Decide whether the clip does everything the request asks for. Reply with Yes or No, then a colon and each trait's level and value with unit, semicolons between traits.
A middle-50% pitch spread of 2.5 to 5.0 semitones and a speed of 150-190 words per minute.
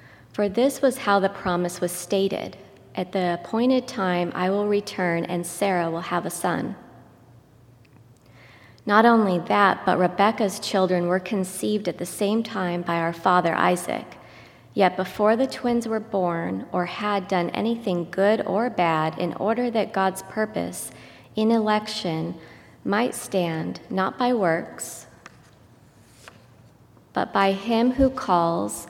No: average, 3.8 semitones; average, 140 wpm